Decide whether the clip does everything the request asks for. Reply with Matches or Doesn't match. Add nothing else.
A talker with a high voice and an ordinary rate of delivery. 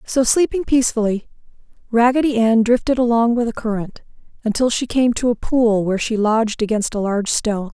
Matches